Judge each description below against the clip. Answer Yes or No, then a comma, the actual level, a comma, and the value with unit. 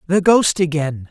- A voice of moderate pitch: Yes, medium, 165 Hz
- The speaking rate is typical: Yes, average, 165 wpm